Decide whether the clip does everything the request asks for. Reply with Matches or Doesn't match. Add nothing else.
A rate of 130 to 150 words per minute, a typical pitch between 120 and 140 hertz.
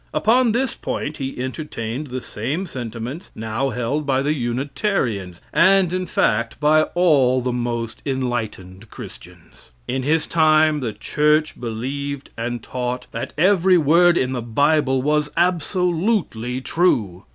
Matches